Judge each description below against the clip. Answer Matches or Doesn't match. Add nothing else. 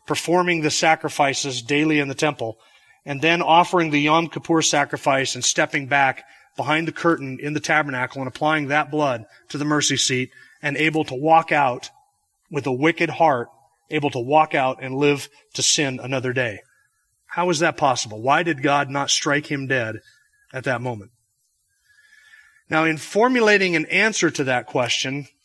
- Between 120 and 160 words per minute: Doesn't match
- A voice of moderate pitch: Matches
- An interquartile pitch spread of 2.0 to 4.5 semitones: Matches